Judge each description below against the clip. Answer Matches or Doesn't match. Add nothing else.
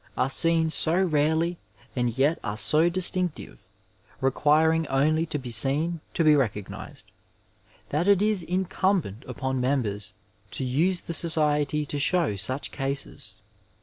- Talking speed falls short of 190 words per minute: Matches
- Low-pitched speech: Doesn't match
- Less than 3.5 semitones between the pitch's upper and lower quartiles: Doesn't match